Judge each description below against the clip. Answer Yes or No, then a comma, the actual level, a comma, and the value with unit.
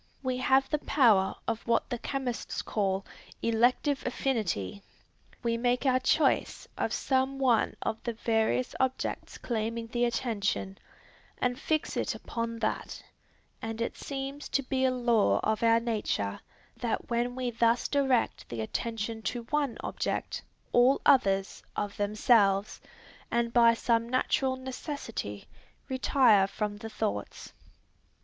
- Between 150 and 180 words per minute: No, slow, 135 wpm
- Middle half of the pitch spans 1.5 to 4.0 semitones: Yes, average, 2.9 semitones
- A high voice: Yes, high, 235 Hz